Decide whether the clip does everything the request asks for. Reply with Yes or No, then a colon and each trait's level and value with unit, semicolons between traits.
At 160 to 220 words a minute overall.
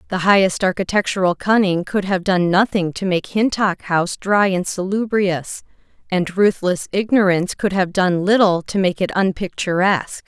No: average, 150 wpm